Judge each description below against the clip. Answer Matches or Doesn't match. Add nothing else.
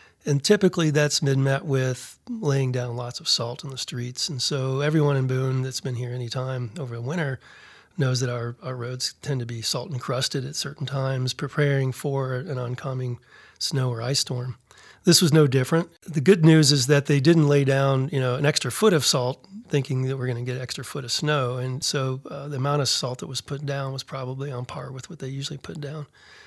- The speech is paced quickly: Matches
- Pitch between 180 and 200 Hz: Doesn't match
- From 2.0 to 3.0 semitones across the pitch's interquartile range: Matches